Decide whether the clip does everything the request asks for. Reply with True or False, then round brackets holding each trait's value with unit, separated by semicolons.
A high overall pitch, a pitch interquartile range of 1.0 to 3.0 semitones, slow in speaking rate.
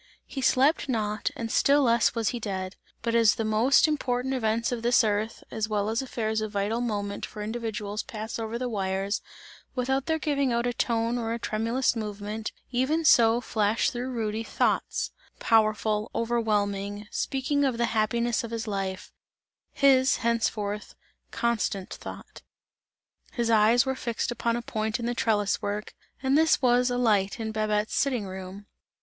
False (225 Hz; 2.5 semitones; 165 wpm)